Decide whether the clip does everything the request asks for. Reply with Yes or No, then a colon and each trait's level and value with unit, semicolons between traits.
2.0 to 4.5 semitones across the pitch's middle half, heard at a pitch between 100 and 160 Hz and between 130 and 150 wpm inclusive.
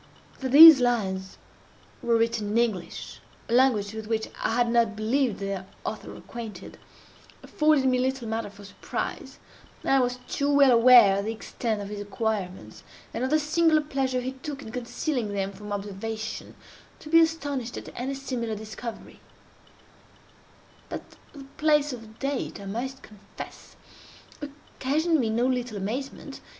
No: average, 4.0 semitones; high, 240 Hz; average, 145 wpm